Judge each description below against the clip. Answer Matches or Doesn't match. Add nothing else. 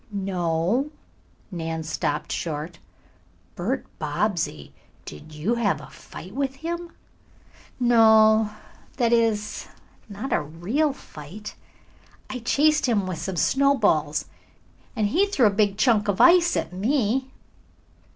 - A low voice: Doesn't match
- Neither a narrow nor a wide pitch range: Doesn't match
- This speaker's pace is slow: Matches